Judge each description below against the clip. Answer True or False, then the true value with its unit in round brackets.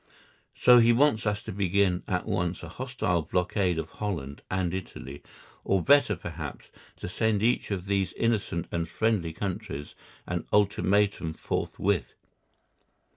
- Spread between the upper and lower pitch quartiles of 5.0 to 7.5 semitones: False (3.5 semitones)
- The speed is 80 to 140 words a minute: True (135 wpm)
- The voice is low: True (95 Hz)